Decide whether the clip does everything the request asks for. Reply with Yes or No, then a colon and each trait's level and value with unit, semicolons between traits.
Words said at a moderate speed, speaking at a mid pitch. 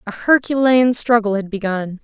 No: average, 145 wpm; high, 225 Hz